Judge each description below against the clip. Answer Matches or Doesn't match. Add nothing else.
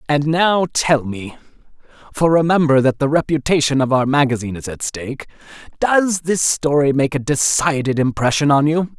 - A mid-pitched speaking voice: Matches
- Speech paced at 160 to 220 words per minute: Doesn't match